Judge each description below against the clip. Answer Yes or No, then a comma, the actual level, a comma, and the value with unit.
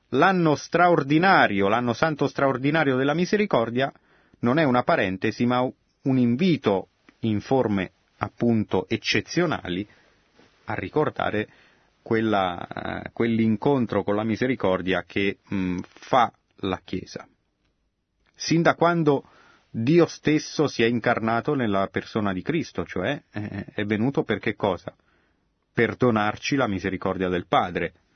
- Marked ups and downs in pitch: Yes, wide, 6.0 semitones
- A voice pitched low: Yes, low, 115 Hz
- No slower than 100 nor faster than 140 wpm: Yes, average, 120 wpm